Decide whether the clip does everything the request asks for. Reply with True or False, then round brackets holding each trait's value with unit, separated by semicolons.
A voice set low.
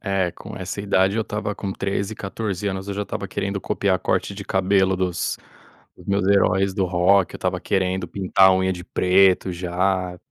True (95 Hz)